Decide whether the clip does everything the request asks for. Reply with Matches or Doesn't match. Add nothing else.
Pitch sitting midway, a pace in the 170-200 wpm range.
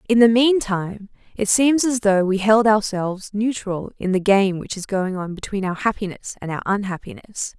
Doesn't match